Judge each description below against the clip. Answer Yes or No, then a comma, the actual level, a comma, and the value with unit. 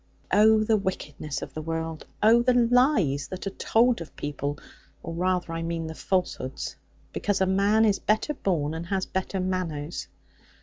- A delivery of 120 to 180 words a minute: Yes, average, 170 wpm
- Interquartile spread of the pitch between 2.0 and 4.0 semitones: No, average, 4.7 semitones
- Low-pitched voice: No, medium, 185 Hz